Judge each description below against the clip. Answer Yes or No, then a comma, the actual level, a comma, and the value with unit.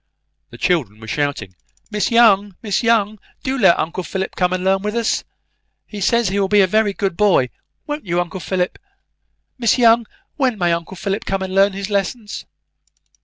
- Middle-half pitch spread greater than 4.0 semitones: No, average, 3.1 semitones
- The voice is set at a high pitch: Yes, high, 195 Hz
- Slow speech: No, average, 185 wpm